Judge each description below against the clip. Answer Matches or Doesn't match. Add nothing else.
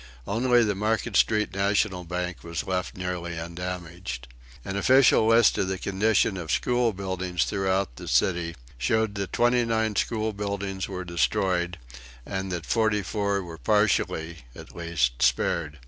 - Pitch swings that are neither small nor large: Matches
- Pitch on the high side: Doesn't match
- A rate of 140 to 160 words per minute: Matches